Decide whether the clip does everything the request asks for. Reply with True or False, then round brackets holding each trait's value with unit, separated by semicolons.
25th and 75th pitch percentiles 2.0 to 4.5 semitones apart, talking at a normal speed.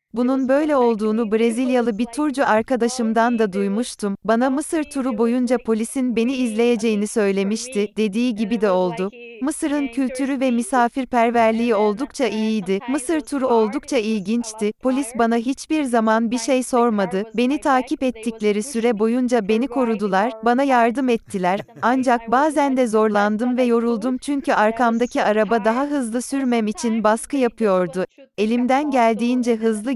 True (2.9 semitones; 130 wpm)